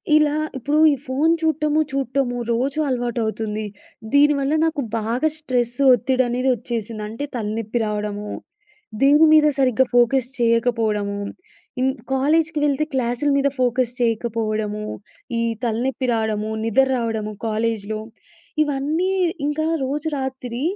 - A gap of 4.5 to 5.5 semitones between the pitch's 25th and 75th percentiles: No, average, 3.9 semitones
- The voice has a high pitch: Yes, high, 245 Hz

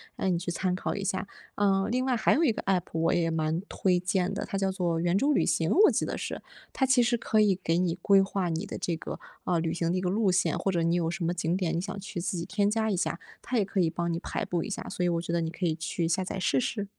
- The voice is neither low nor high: Yes, medium, 180 Hz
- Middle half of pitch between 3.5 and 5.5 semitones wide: No, average, 2.8 semitones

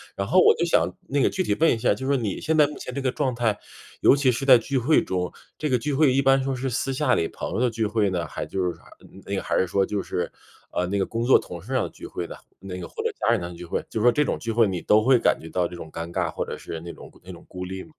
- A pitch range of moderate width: No, wide, 6.4 semitones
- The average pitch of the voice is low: Yes, low, 115 Hz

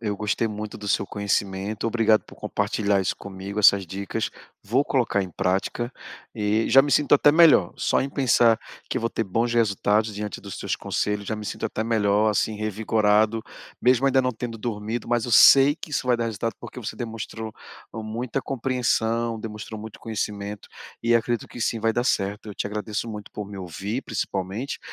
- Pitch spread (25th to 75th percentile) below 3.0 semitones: Yes, narrow, 2.4 semitones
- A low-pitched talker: Yes, low, 110 Hz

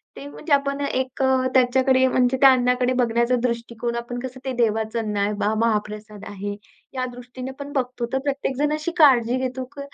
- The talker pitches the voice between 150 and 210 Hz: No, very high, 250 Hz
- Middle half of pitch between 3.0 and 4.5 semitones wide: No, narrow, 2.4 semitones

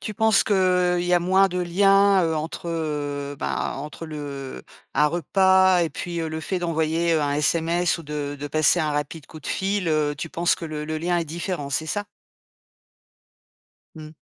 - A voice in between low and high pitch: Yes, medium, 165 Hz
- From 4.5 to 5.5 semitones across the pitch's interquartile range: No, average, 3.1 semitones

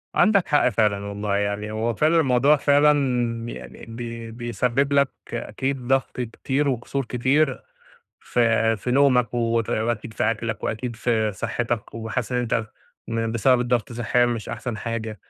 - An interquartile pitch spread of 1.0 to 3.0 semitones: Yes, narrow, 2.6 semitones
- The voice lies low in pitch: Yes, low, 120 Hz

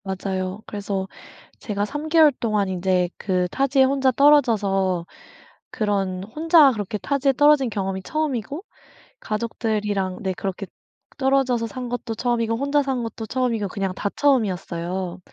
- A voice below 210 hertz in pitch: No, high, 220 Hz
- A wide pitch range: Yes, wide, 5.7 semitones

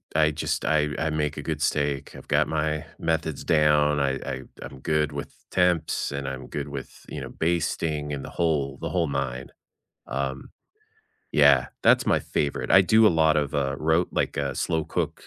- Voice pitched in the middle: No, very low, 75 Hz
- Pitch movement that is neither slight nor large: No, narrow, 2.3 semitones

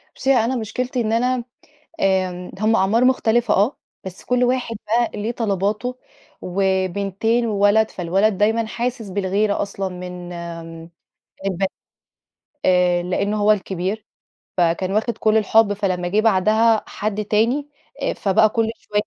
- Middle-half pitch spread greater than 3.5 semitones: No, average, 3.2 semitones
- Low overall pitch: No, high, 210 Hz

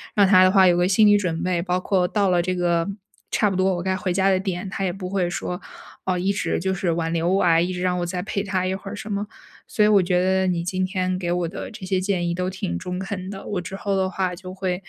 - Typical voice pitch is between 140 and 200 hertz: Yes, medium, 185 Hz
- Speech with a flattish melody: Yes, narrow, 1.5 semitones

